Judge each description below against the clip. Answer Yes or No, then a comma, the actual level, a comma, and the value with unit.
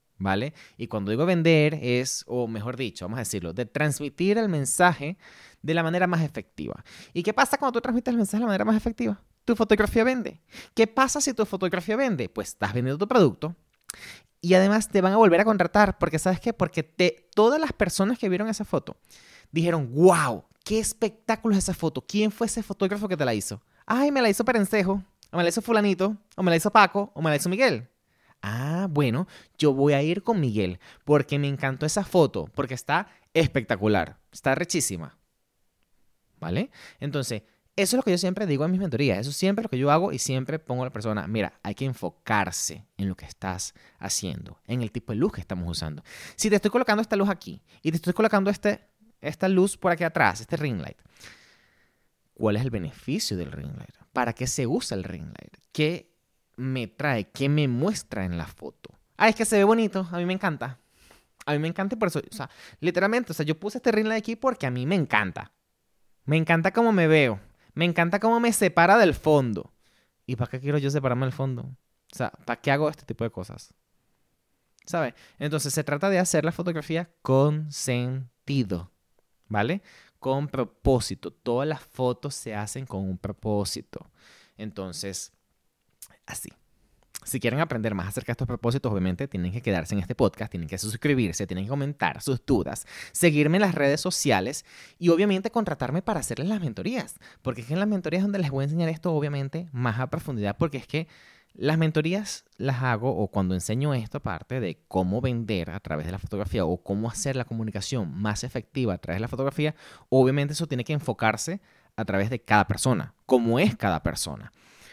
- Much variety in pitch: Yes, wide, 8.6 semitones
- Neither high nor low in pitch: Yes, medium, 145 Hz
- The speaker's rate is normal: No, fast, 205 wpm